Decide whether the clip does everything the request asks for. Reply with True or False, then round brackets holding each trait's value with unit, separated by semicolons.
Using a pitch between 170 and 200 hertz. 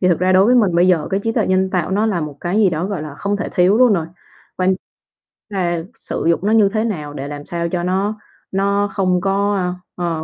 True (185 Hz)